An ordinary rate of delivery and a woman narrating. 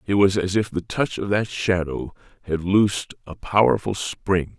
No: average, 185 wpm; male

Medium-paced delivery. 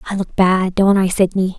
No: fast, 225 wpm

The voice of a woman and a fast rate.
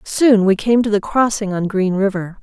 Yes: female; fast, 225 wpm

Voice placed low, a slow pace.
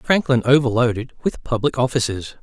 Yes: low, 120 Hz; slow, 125 wpm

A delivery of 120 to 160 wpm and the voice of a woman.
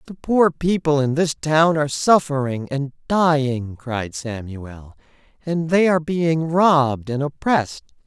No: average, 140 wpm; male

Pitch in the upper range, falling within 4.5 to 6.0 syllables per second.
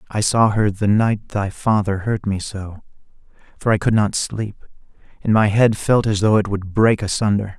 No: low, 105 Hz; 4.6 syllables/s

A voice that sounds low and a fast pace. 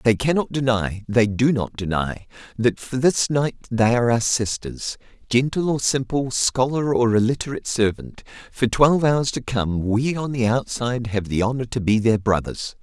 No: low, 120 Hz; average, 165 wpm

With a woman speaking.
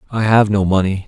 No: male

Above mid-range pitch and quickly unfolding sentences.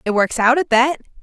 Yes: very high, 250 Hz; fast, 245 wpm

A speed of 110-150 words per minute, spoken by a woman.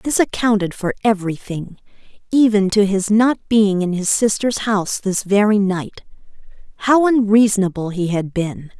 Yes: average, 145 wpm; female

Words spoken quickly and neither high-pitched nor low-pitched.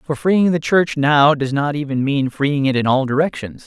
Yes: fast, 230 wpm; medium, 145 Hz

